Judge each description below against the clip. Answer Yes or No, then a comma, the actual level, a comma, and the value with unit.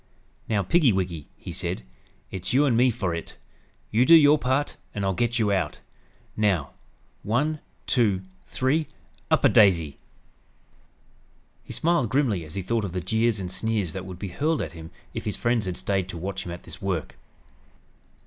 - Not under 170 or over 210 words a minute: Yes, average, 180 wpm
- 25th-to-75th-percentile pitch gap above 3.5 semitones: Yes, average, 5.2 semitones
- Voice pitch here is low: Yes, low, 105 Hz